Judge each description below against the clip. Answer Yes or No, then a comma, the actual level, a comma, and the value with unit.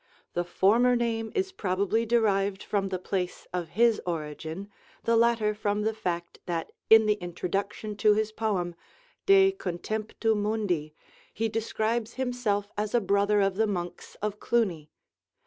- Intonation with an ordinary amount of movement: Yes, average, 3.4 semitones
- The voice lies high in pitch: Yes, high, 210 Hz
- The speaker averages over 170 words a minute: No, average, 145 wpm